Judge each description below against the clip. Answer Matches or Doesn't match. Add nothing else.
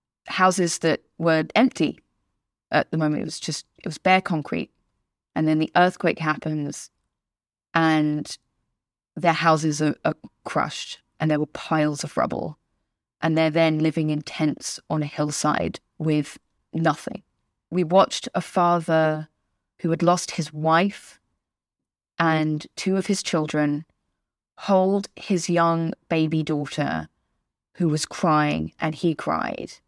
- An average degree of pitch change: Doesn't match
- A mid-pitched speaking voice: Matches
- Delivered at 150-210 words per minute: Doesn't match